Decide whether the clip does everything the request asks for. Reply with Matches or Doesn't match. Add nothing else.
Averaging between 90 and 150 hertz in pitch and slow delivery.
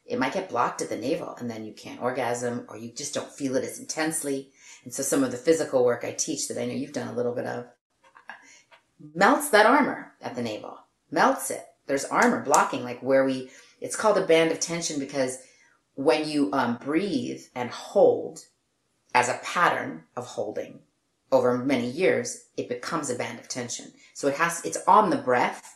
Doesn't match